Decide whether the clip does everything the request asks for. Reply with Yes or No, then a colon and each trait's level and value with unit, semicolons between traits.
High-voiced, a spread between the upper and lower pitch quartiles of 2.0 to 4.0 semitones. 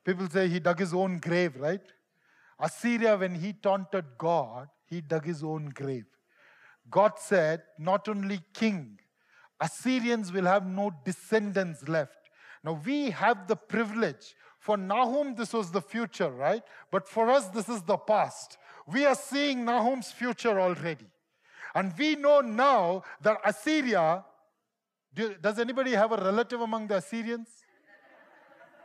No: high, 200 Hz; average, 5.0 semitones